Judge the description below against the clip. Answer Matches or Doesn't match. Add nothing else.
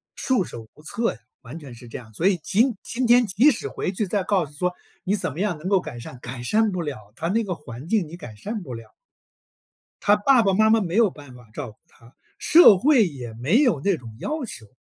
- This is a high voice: Doesn't match